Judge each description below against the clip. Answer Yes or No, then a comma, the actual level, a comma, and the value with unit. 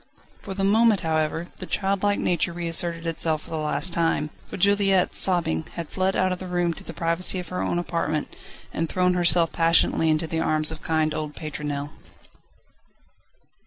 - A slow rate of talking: No, average, 175 wpm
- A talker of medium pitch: Yes, medium, 170 Hz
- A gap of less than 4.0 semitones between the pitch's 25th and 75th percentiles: Yes, narrow, 2.5 semitones